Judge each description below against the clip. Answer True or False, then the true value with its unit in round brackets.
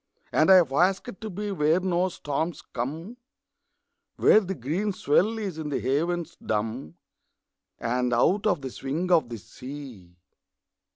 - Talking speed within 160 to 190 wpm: False (150 wpm)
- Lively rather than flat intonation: True (6.4 semitones)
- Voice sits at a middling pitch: True (160 Hz)